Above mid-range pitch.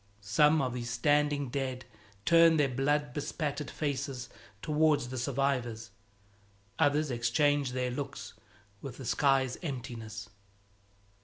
No: low, 135 Hz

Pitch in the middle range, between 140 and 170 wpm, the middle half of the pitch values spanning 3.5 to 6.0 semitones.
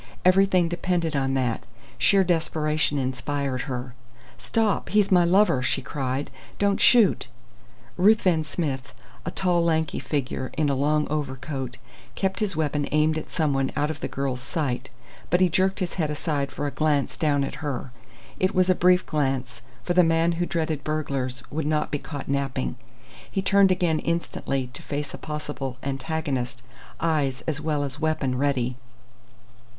Yes: medium, 150 Hz; average, 165 wpm; average, 4.0 semitones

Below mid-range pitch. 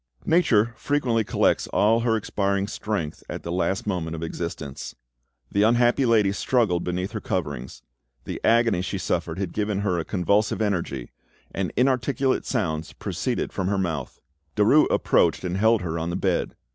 Yes: low, 100 Hz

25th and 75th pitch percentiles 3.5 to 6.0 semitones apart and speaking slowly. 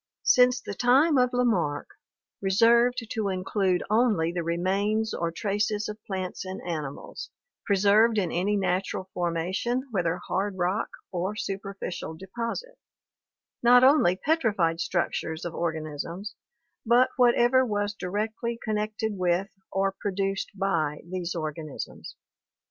Yes: average, 4.2 semitones; slow, 120 wpm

